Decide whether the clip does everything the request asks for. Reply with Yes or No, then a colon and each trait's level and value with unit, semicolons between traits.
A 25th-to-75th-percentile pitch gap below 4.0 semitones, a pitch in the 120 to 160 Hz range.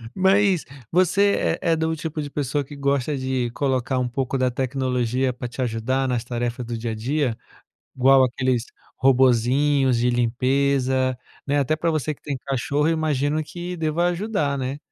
Yes: average, 3.3 semitones; low, 135 Hz